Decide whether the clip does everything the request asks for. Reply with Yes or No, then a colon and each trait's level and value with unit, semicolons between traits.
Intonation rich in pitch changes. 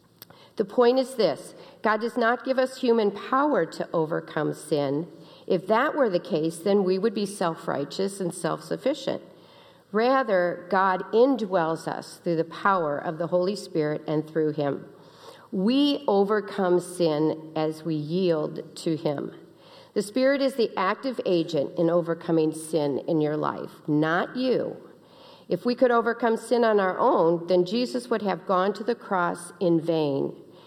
Yes: wide, 5.7 semitones